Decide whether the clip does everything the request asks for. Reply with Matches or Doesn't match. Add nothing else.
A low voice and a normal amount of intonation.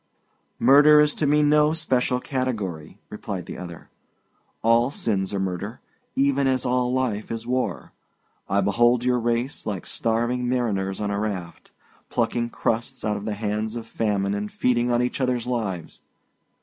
Matches